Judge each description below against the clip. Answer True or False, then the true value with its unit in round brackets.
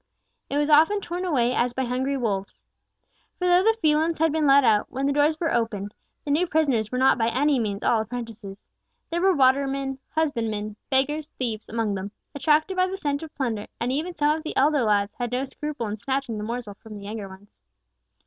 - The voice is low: False (265 Hz)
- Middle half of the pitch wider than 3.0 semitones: True (5.2 semitones)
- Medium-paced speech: False (210 wpm)